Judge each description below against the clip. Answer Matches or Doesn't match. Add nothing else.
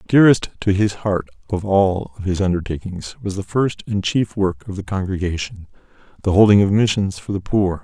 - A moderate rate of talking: Matches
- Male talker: Matches